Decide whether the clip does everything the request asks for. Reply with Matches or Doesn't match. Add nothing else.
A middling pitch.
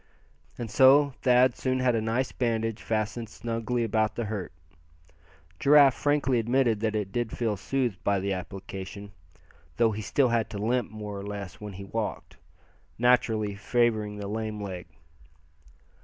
Doesn't match